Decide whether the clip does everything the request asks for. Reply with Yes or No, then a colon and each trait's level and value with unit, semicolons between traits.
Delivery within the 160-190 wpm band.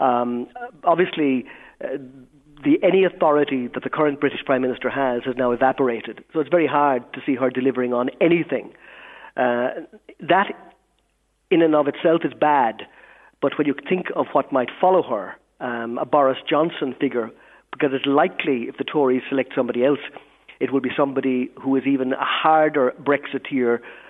Yes: average, 165 wpm